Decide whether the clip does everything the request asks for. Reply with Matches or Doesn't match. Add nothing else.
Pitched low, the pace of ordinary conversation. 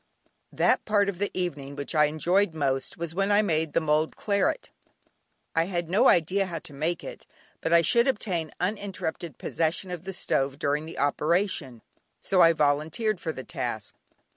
Doesn't match